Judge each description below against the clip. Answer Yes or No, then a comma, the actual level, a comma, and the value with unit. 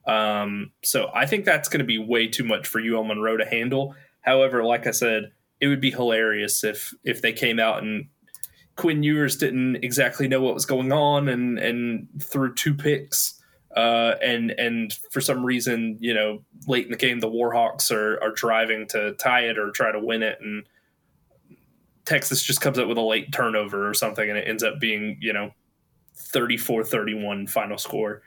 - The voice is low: Yes, low, 115 Hz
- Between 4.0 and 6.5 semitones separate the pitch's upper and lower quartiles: No, average, 3.2 semitones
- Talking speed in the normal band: Yes, average, 195 wpm